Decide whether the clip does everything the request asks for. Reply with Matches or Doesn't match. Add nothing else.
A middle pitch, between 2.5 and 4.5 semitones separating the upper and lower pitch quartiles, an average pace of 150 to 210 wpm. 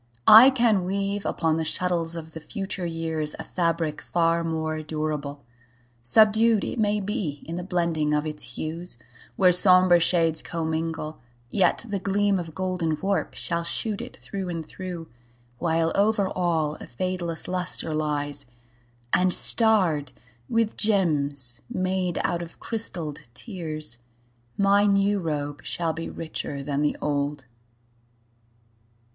Doesn't match